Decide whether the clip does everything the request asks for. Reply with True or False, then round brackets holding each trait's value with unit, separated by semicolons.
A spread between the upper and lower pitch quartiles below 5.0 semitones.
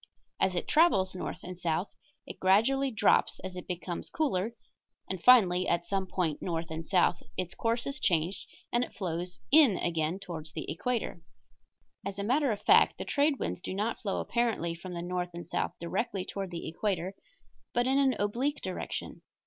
False (5.3 semitones)